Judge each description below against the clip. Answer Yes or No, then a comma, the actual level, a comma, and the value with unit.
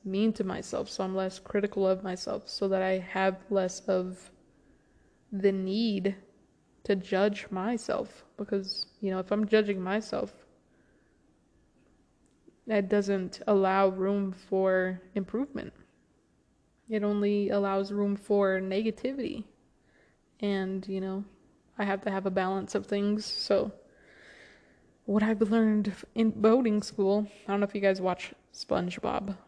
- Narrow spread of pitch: Yes, narrow, 1.6 semitones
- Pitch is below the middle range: No, high, 200 Hz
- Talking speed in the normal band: No, slow, 130 wpm